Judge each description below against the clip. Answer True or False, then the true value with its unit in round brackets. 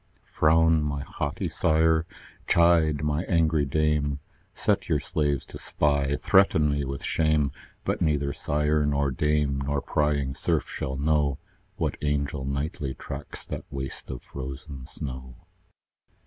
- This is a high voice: False (75 Hz)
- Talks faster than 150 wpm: False (135 wpm)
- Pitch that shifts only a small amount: True (1.8 semitones)